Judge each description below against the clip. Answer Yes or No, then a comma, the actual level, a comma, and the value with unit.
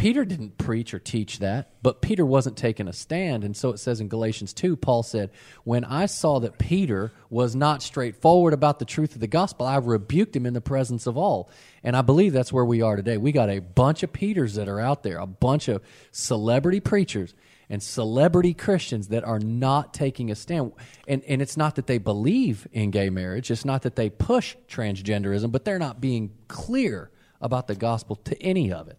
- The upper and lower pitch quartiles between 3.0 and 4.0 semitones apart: No, average, 5.0 semitones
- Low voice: Yes, low, 125 Hz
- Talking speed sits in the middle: No, fast, 215 wpm